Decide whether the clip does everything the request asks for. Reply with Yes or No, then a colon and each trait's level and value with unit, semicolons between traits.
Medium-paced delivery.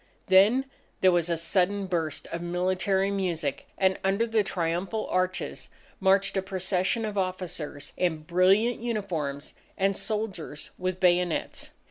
No: slow, 130 wpm